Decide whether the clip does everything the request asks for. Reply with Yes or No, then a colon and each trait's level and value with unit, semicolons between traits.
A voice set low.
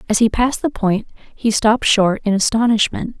No: high, 220 Hz